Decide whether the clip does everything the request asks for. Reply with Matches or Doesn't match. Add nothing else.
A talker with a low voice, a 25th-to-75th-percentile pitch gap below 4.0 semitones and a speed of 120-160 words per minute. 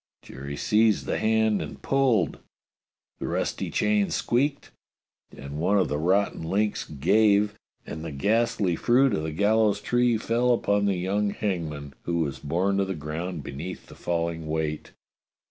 Doesn't match